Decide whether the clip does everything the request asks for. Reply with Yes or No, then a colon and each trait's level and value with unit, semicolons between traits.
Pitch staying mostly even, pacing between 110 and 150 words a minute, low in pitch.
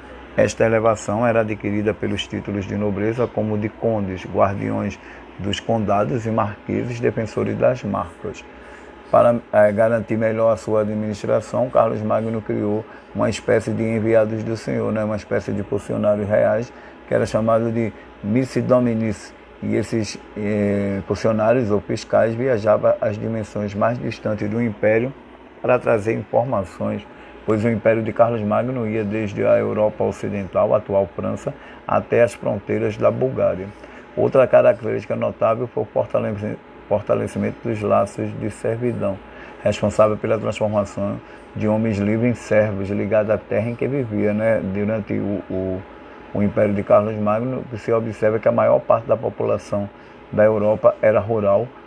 Yes: narrow, 1.6 semitones; average, 145 wpm; low, 110 Hz